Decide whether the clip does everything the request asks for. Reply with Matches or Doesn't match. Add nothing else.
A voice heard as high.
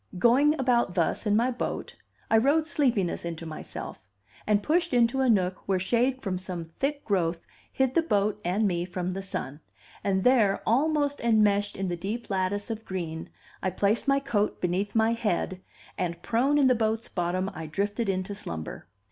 Matches